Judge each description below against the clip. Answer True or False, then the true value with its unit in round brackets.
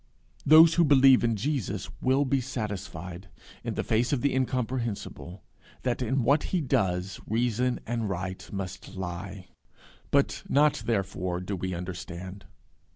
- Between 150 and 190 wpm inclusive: False (140 wpm)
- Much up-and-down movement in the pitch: True (5.8 semitones)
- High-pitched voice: False (110 Hz)